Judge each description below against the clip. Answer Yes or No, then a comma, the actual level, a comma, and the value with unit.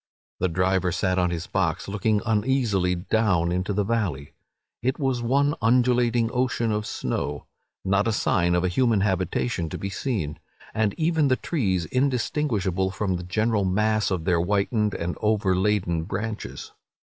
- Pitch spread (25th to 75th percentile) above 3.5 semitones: Yes, average, 4.1 semitones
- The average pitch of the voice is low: Yes, low, 100 Hz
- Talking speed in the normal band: Yes, average, 150 wpm